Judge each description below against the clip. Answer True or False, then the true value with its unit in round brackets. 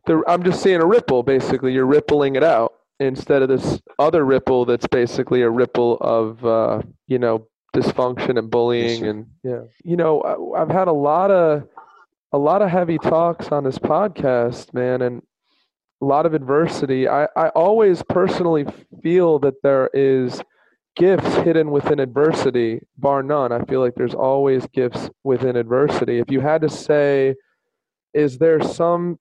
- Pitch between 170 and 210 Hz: False (135 Hz)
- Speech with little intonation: False (4.0 semitones)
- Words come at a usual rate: True (160 wpm)